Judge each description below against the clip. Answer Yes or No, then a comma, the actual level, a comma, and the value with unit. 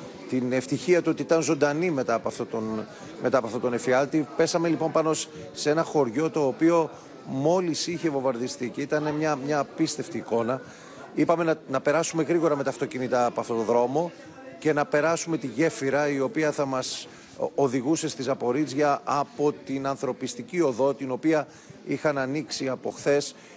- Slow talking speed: No, fast, 170 wpm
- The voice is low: No, medium, 145 Hz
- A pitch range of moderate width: Yes, average, 3.3 semitones